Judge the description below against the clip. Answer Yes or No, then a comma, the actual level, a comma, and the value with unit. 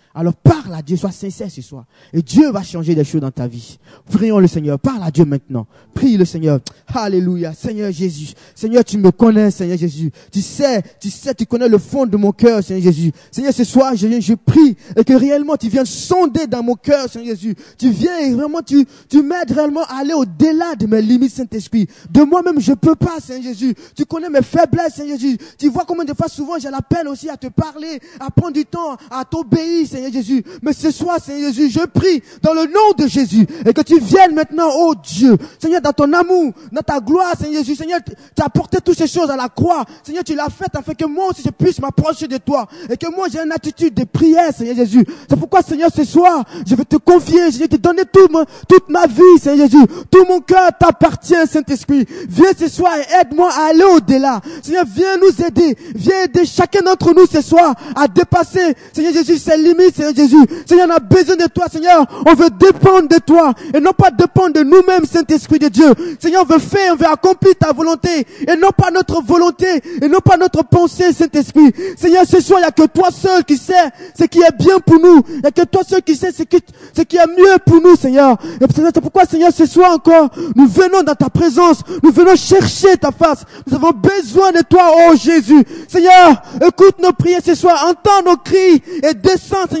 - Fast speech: Yes, fast, 225 wpm